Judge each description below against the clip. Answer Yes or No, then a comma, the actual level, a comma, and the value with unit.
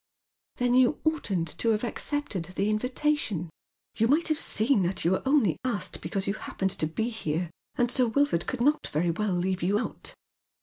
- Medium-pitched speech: No, high, 215 Hz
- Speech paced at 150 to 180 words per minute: No, average, 190 wpm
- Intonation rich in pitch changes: Yes, wide, 5.9 semitones